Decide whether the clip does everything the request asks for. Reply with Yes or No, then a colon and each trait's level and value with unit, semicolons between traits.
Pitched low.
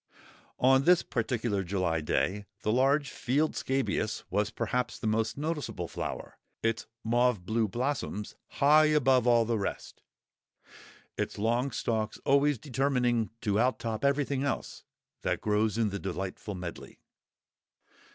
Yes: low, 120 Hz